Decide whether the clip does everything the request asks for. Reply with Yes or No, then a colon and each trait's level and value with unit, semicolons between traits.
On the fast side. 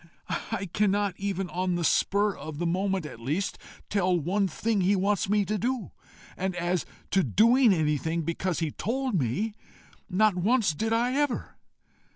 No: average, 165 wpm